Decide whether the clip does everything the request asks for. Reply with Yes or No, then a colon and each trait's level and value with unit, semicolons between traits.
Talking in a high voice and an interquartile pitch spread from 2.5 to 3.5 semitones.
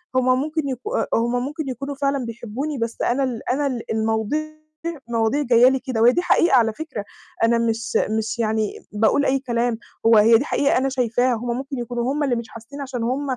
Yes: high, 245 Hz; average, 3.0 semitones